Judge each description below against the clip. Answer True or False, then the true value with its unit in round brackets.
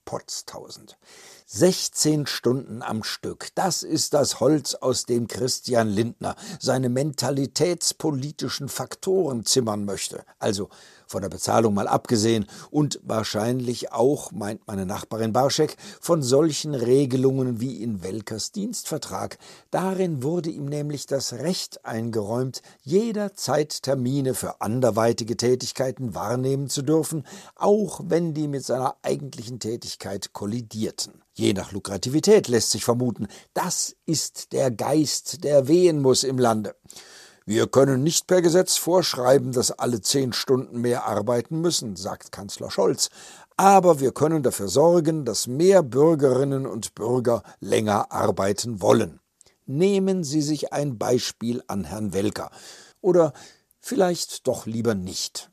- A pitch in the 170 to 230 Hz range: False (130 Hz)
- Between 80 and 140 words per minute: True (130 wpm)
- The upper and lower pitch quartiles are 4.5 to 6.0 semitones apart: True (5.2 semitones)